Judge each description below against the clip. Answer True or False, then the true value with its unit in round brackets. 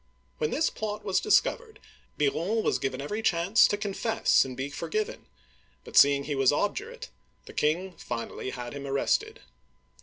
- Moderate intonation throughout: False (7.9 semitones)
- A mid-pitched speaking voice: True (175 Hz)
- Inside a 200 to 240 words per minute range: False (160 wpm)